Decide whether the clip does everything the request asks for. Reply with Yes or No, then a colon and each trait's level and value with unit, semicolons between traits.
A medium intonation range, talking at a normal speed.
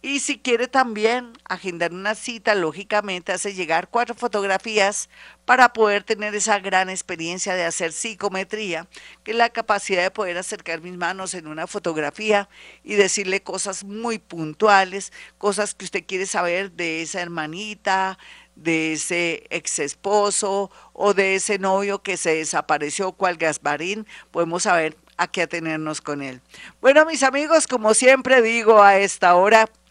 Yes: average, 3.6 semitones; average, 150 wpm